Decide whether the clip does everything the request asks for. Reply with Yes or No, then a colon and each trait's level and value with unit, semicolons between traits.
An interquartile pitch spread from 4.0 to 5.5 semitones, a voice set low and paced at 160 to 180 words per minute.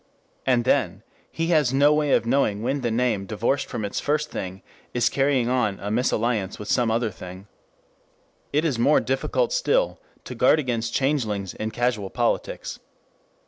Yes: average, 4.5 semitones; low, 120 Hz; average, 165 wpm